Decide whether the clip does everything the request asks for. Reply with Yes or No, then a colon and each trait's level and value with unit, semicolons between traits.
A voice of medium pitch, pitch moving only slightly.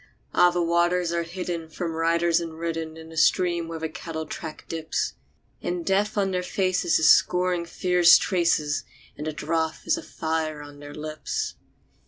Yes: medium, 165 Hz; narrow, 1.9 semitones